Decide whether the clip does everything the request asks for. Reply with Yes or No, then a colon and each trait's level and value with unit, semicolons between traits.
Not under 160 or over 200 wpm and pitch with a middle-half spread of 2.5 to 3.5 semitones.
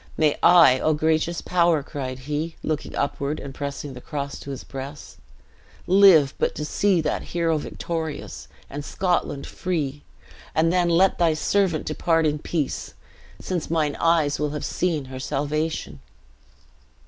No: average, 150 wpm; average, 2.9 semitones